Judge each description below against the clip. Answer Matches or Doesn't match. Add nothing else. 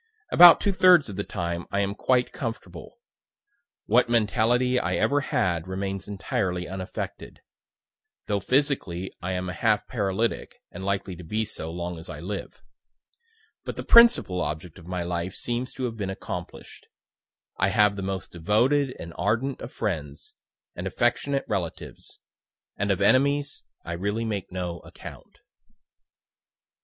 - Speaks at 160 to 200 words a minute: Doesn't match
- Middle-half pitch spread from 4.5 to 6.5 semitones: Matches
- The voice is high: Doesn't match